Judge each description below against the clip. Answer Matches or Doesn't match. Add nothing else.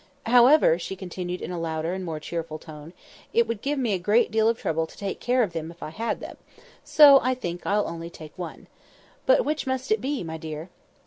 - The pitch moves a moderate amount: Doesn't match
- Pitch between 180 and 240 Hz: Matches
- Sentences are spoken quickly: Matches